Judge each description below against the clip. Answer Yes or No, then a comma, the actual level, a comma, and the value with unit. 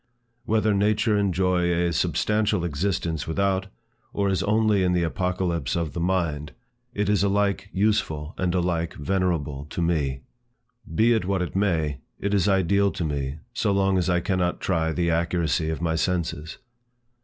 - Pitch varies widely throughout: No, average, 3.2 semitones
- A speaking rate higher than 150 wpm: Yes, average, 160 wpm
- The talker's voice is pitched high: No, very low, 90 Hz